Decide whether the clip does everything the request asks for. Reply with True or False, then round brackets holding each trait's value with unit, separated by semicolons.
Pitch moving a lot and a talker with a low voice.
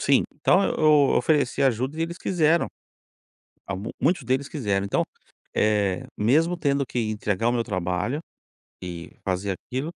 True (6.9 semitones; 125 Hz)